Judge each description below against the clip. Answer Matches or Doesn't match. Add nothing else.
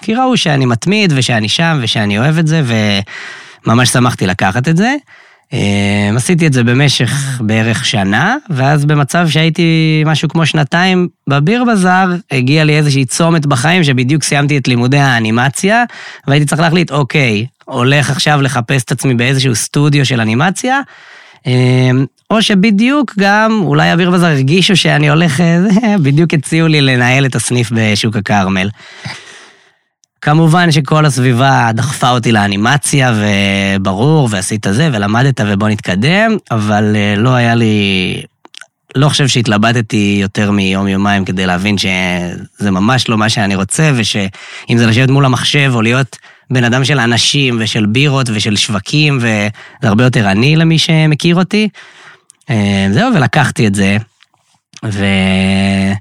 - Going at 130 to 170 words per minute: Matches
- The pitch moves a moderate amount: Doesn't match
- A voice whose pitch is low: Matches